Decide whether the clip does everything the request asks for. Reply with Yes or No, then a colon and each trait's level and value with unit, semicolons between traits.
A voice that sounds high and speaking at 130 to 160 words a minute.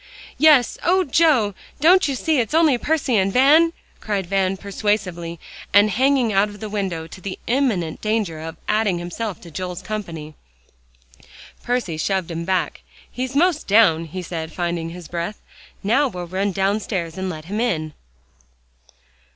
Yes: high, 195 Hz; average, 155 wpm